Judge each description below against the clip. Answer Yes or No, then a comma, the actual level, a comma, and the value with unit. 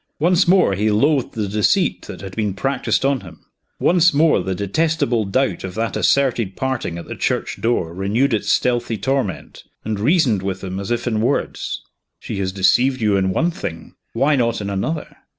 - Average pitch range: No, wide, 5.9 semitones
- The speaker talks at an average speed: Yes, average, 185 wpm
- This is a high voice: No, low, 115 Hz